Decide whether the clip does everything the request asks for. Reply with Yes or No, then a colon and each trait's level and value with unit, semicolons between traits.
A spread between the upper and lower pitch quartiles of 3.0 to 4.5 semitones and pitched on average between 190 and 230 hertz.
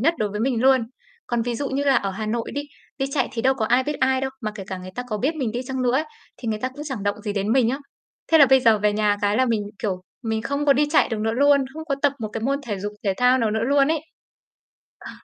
No: average, 4.0 semitones; high, 245 Hz